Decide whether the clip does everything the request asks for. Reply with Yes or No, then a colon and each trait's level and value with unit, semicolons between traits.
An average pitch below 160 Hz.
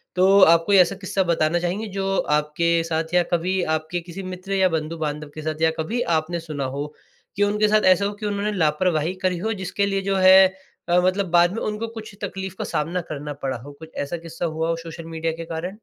No: medium, 175 Hz